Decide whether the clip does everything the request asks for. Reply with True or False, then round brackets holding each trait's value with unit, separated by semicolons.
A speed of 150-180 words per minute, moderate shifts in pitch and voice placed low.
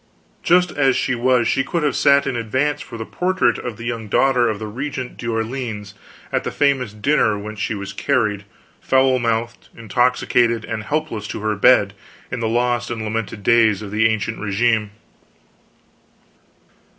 True (165 wpm; 3.2 semitones; 115 Hz)